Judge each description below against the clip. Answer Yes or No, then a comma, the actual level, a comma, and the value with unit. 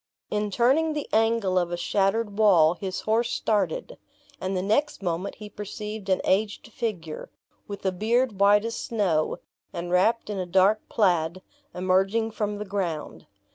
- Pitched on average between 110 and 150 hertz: No, high, 205 Hz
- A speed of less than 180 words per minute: Yes, average, 160 wpm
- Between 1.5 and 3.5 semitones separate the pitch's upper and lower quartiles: Yes, average, 3.1 semitones